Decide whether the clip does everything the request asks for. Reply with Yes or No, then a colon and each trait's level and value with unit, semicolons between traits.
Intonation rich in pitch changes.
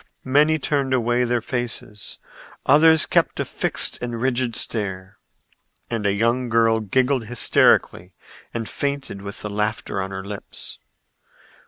No: average, 3.8 semitones